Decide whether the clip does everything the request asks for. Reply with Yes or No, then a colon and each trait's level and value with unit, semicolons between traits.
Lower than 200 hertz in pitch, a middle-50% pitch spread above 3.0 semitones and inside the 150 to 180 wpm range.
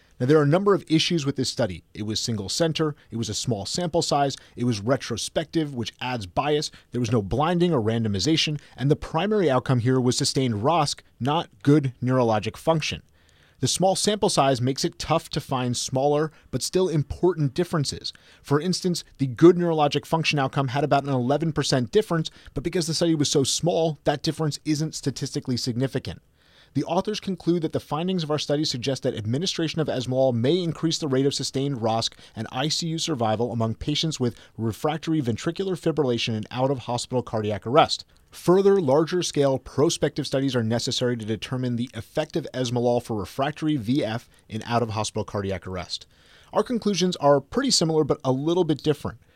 Yes: medium, 140 Hz; average, 4.9 semitones; average, 175 wpm